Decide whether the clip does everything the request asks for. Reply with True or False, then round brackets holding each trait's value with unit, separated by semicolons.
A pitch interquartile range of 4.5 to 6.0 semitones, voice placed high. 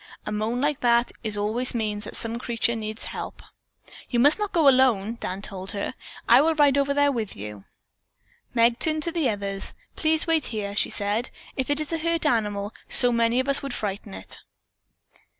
True (5.4 semitones; 235 Hz)